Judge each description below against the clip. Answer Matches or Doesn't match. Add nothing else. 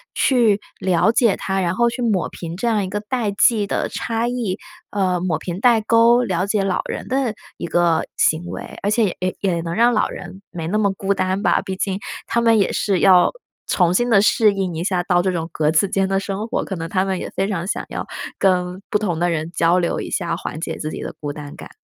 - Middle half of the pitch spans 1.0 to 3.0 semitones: Doesn't match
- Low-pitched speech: Doesn't match